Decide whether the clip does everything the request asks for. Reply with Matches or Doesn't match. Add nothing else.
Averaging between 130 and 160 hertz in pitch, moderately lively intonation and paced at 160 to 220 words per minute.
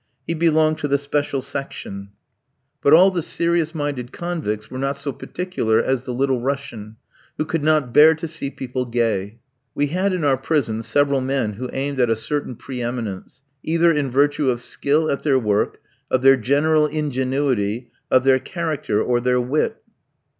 Matches